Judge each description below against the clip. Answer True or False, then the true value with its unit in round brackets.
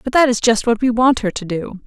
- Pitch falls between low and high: False (230 Hz)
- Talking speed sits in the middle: False (320 wpm)